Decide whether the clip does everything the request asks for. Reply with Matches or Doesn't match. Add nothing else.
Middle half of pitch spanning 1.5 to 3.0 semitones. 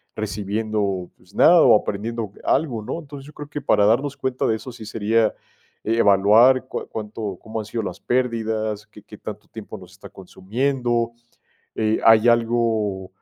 Matches